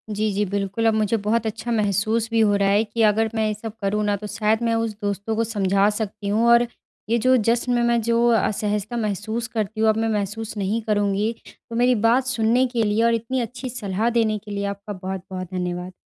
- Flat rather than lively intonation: Yes, narrow, 2.1 semitones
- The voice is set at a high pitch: Yes, high, 215 Hz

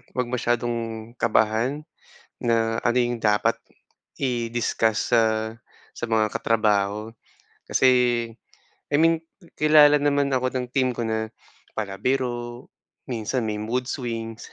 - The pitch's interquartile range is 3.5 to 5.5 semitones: No, narrow, 2.4 semitones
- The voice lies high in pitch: No, low, 120 Hz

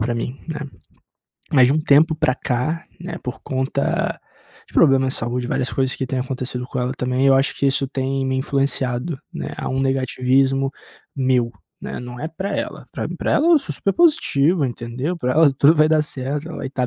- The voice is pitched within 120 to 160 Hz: Yes, low, 135 Hz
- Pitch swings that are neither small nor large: Yes, average, 3.0 semitones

